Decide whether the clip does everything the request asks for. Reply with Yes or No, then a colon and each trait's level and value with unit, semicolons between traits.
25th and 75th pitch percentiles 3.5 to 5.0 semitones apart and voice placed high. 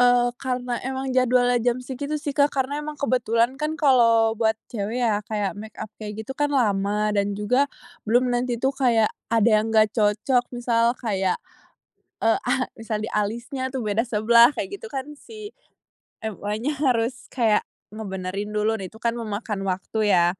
No: average, 3.1 semitones; high, 230 Hz